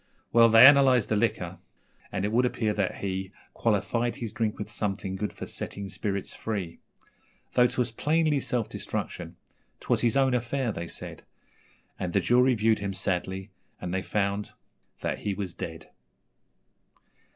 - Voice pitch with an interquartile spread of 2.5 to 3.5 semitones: No, average, 4.0 semitones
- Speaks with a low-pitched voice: Yes, low, 105 Hz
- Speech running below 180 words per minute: Yes, average, 155 wpm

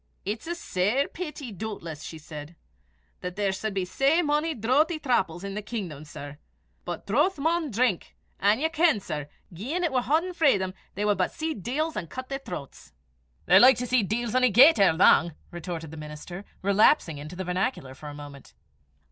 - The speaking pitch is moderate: No, high, 210 Hz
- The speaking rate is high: No, average, 190 wpm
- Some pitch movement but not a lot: No, wide, 8.0 semitones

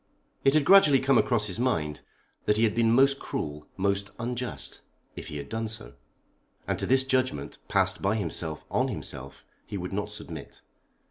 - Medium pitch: No, low, 105 Hz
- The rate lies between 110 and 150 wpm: No, average, 180 wpm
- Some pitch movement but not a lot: No, wide, 6.4 semitones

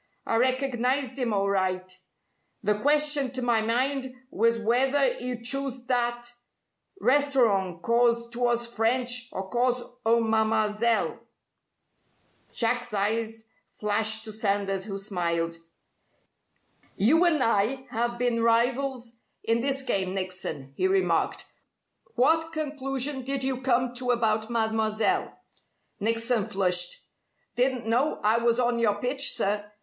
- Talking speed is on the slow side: Yes, slow, 120 wpm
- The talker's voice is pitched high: Yes, high, 235 Hz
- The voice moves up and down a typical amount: Yes, average, 3.1 semitones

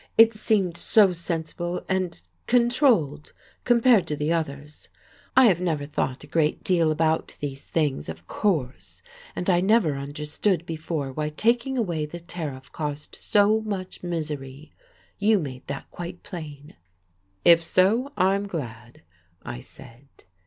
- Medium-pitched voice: Yes, medium, 165 Hz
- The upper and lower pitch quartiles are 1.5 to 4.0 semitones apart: No, average, 5.1 semitones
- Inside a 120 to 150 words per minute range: Yes, average, 140 wpm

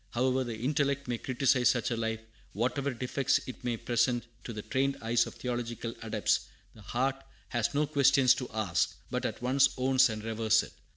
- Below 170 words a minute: No, average, 185 wpm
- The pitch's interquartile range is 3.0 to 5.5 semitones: No, narrow, 2.6 semitones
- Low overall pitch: Yes, low, 125 Hz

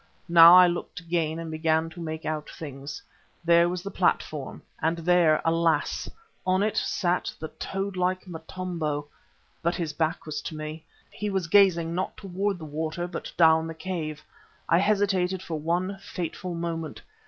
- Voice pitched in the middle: Yes, medium, 170 Hz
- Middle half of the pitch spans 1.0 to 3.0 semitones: Yes, narrow, 2.4 semitones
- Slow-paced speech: No, average, 165 wpm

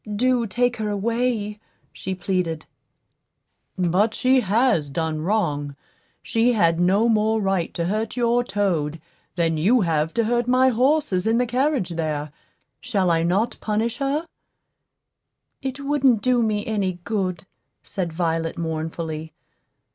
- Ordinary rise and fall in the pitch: No, wide, 6.1 semitones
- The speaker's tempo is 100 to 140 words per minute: Yes, slow, 135 wpm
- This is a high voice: Yes, high, 205 Hz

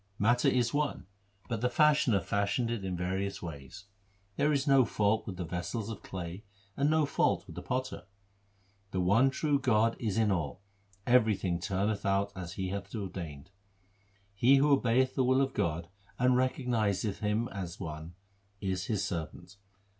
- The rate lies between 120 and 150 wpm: No, average, 170 wpm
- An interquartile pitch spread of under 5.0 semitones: No, average, 5.3 semitones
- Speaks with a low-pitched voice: Yes, low, 105 Hz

